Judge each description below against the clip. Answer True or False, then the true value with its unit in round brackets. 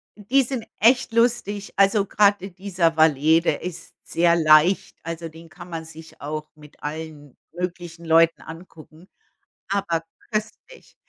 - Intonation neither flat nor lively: True (3.8 semitones)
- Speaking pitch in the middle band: True (170 Hz)